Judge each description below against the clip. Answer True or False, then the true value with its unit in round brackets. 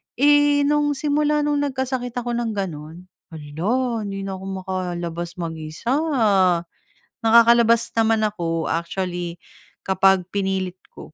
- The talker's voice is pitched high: True (195 Hz)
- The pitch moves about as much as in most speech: False (5.9 semitones)